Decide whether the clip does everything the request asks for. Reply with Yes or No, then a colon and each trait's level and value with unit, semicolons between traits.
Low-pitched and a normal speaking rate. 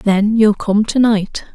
No: high, 210 Hz; average, 195 wpm